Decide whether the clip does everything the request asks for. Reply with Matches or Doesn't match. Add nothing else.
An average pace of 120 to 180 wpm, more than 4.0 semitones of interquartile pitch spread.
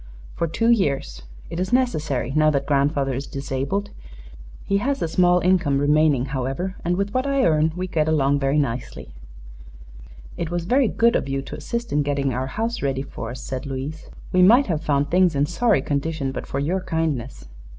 Doesn't match